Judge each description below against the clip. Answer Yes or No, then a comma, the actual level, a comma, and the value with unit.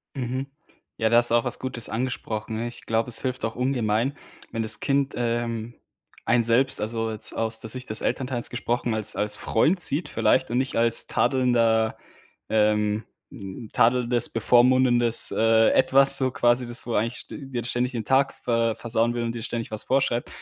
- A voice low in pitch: Yes, low, 120 Hz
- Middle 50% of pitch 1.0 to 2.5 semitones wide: Yes, narrow, 2.1 semitones